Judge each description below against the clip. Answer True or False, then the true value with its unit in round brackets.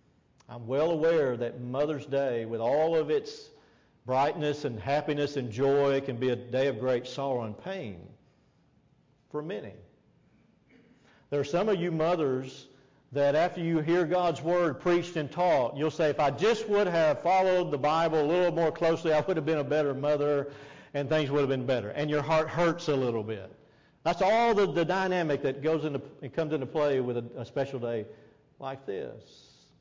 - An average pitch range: True (3.7 semitones)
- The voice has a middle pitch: True (145 Hz)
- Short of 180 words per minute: False (190 wpm)